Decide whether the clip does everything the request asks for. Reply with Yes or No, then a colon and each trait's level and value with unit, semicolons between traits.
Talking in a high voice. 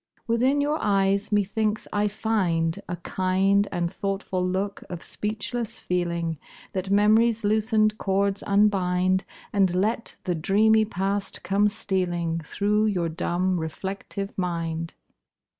Yes: high, 195 Hz